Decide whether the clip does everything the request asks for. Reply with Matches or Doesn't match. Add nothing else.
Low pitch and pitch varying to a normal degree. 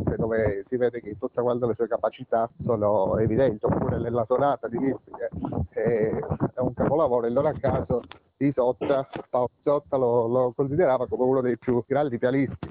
Doesn't match